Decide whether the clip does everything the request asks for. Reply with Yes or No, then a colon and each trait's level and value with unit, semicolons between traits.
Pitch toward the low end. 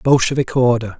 Yes: low, 120 Hz